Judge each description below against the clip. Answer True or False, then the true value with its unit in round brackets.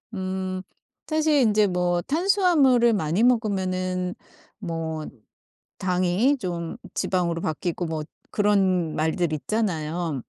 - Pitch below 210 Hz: True (185 Hz)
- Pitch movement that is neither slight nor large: True (4.2 semitones)